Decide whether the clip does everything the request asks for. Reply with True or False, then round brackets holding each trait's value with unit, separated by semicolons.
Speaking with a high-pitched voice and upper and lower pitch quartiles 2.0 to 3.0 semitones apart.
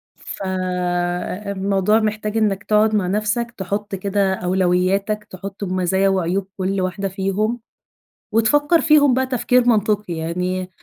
True (195 Hz; 2.5 semitones)